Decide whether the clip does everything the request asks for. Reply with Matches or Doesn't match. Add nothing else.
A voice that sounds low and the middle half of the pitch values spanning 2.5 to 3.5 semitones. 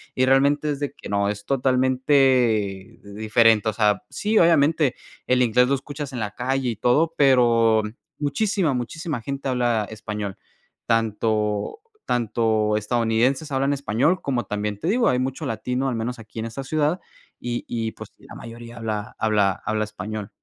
Doesn't match